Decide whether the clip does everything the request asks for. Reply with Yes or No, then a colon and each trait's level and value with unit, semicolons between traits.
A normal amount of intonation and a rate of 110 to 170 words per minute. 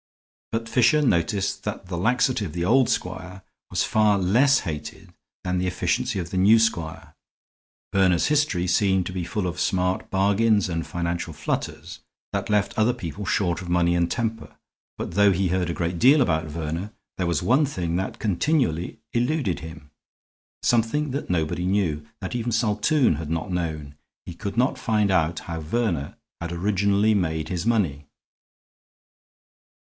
Yes: average, 4.6 semitones; average, 165 wpm